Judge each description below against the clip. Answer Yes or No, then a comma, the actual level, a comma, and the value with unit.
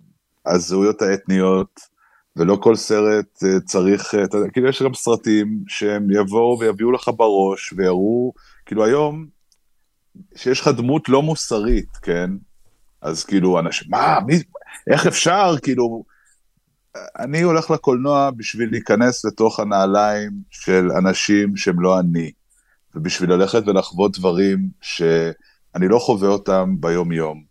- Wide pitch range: No, average, 4.4 semitones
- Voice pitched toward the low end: Yes, low, 105 Hz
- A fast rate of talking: No, average, 120 wpm